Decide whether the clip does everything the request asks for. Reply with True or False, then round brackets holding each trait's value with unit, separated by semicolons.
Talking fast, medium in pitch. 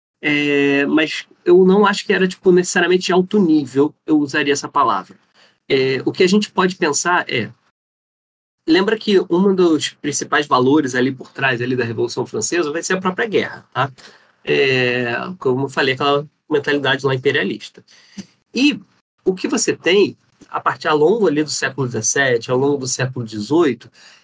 False (170 wpm; 150 Hz)